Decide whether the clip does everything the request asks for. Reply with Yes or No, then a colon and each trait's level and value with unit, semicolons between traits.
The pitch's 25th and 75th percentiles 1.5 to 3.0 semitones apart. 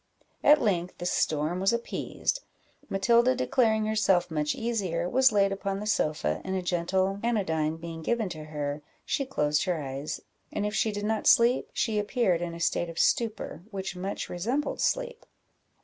No: average, 5.1 semitones